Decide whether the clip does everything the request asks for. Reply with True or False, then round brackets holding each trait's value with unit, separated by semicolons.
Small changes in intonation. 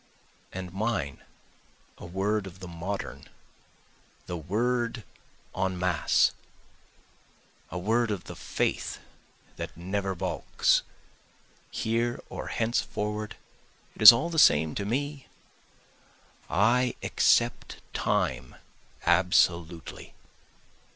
False (4.7 semitones)